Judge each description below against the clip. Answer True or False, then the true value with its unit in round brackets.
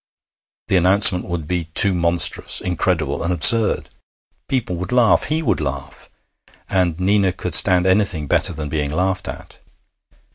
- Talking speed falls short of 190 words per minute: True (145 wpm)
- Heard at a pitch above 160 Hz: False (90 Hz)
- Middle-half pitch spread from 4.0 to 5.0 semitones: False (2.9 semitones)